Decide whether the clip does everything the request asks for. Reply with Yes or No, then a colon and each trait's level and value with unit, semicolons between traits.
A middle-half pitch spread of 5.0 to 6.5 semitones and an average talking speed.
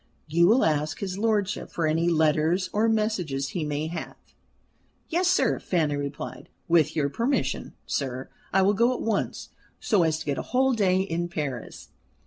Yes: wide, 5.5 semitones; average, 170 wpm